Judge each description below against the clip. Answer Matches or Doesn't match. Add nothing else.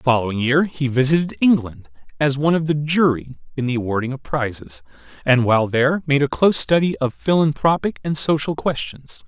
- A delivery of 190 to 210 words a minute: Doesn't match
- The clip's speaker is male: Matches